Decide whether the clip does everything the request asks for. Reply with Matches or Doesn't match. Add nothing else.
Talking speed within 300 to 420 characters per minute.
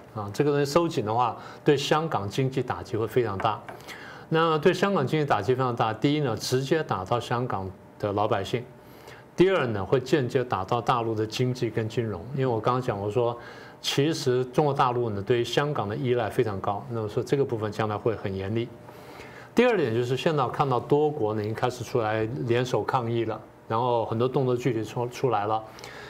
Matches